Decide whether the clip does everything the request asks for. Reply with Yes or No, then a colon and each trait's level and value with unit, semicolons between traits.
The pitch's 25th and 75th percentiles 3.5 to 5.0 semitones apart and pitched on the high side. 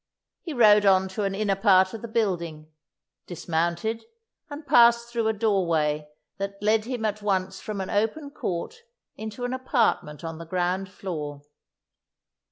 Yes: average, 4.1 semitones; high, 200 Hz